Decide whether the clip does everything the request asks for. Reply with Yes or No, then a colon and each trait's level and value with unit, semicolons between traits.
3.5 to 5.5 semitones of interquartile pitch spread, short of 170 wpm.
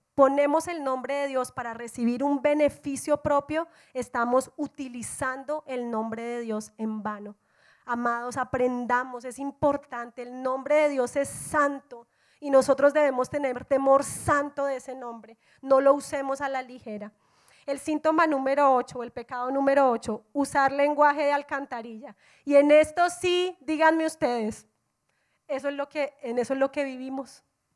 No: average, 2.7 semitones; average, 155 wpm